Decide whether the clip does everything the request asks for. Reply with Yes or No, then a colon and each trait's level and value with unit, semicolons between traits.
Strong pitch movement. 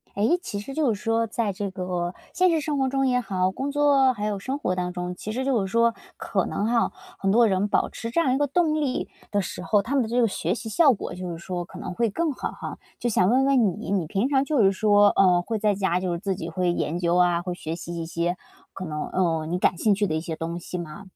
Yes: wide, 5.7 semitones